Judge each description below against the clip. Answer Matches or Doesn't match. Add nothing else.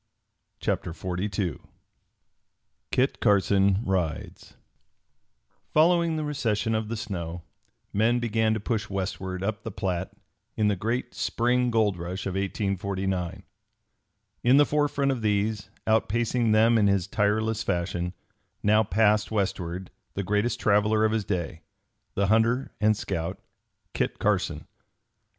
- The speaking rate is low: Matches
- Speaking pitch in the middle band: Doesn't match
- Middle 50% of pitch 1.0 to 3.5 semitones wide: Matches